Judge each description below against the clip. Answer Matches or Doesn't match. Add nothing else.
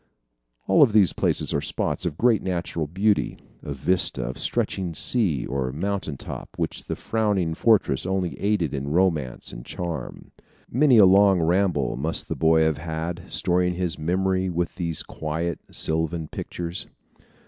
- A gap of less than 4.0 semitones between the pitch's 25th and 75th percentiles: Matches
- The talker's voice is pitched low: Matches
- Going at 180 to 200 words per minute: Doesn't match